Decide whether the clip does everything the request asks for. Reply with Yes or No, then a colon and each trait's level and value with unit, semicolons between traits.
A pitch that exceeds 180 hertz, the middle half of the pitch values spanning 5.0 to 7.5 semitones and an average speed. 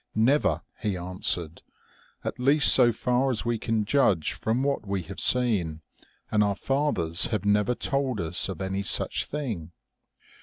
No: low, 105 Hz; average, 5.3 semitones; average, 165 wpm